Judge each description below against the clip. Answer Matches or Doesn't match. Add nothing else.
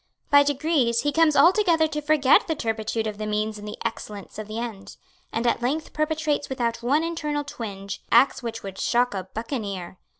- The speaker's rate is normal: Matches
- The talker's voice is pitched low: Doesn't match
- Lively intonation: Matches